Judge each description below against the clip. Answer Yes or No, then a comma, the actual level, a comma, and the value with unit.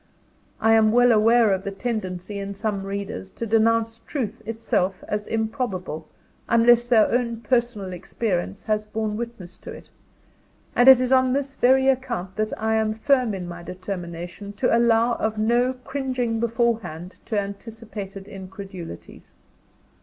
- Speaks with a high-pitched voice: Yes, high, 220 Hz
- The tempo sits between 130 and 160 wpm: Yes, average, 145 wpm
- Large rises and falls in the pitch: No, average, 3.2 semitones